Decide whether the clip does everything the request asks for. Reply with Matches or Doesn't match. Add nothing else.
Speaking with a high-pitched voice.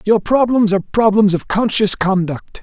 Matches